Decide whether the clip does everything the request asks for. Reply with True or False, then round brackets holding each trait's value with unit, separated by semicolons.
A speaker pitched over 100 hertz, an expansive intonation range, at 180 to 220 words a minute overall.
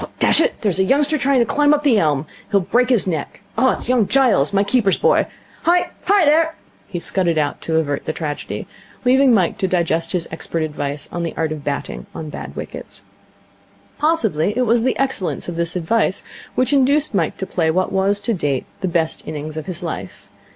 True (190 Hz; 7.9 semitones; 200 wpm)